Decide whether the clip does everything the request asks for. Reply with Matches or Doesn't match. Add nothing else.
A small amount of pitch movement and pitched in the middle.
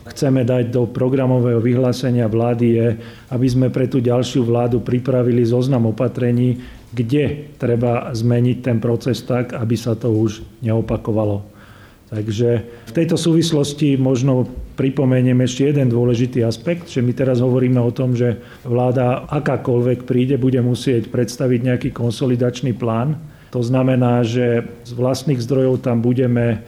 Doesn't match